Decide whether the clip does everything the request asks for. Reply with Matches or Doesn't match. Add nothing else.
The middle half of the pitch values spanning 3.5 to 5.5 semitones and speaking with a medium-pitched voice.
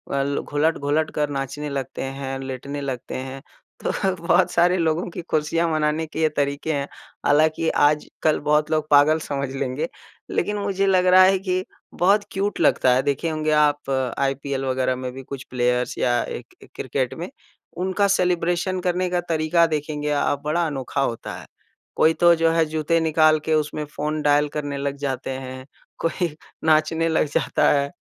Doesn't match